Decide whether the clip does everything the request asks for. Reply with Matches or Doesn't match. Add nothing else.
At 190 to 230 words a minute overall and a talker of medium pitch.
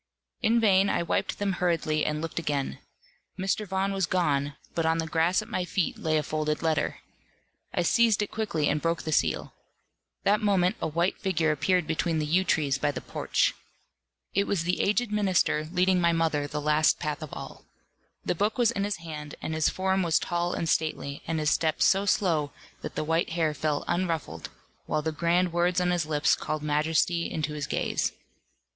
Matches